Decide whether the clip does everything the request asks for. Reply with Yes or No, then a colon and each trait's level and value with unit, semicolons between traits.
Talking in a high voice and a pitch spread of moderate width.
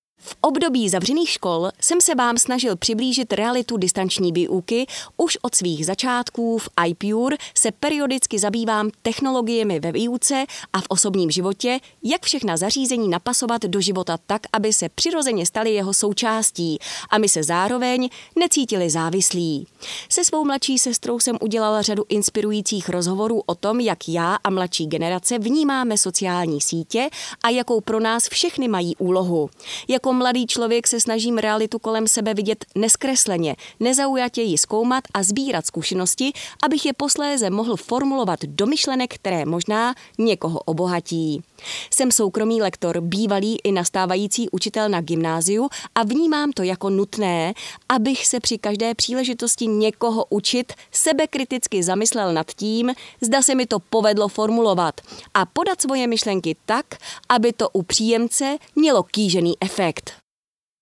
Yes: high, 220 Hz; average, 4.9 semitones